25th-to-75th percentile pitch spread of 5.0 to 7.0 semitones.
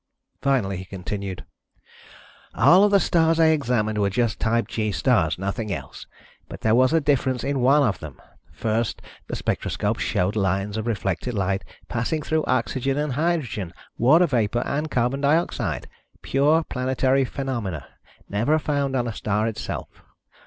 Yes: average, 5.3 semitones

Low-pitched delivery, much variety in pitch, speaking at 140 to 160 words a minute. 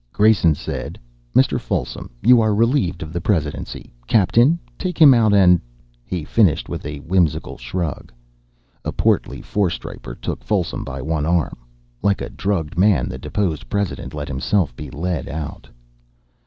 Yes: very low, 85 Hz; wide, 5.7 semitones; average, 155 wpm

